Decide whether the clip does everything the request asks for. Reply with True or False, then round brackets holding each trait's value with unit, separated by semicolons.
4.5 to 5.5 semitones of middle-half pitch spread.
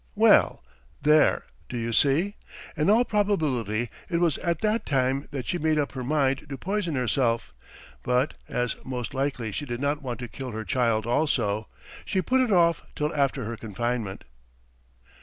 True (4.8 semitones)